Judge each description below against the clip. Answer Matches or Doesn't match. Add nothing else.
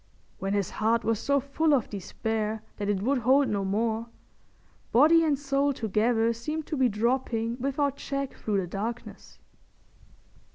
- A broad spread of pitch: Doesn't match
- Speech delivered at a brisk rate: Doesn't match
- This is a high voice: Matches